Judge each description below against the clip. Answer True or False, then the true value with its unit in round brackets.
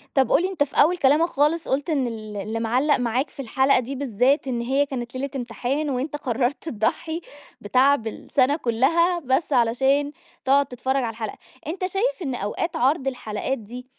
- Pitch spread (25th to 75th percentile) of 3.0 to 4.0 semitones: True (3.3 semitones)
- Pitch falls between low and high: False (265 Hz)